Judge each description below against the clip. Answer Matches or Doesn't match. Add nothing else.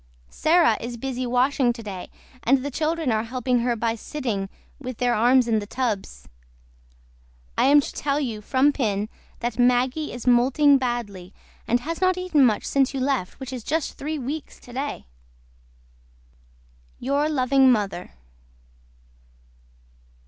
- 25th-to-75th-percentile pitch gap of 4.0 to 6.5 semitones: Doesn't match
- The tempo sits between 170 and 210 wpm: Doesn't match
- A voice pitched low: Doesn't match